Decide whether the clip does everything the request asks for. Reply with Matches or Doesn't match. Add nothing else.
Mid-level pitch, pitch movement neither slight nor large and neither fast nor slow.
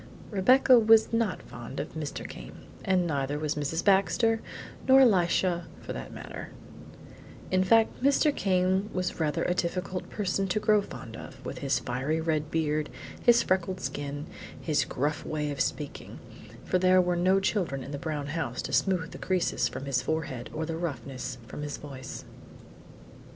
Matches